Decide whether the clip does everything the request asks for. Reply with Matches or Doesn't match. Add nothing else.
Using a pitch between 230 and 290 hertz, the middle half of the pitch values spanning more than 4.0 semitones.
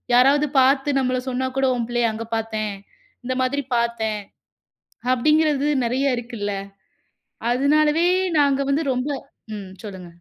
Doesn't match